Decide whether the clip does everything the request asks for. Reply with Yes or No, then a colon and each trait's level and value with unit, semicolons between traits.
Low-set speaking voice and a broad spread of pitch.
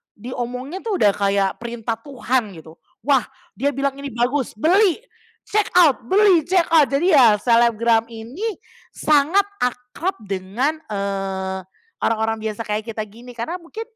No: high, 245 Hz; wide, 6.0 semitones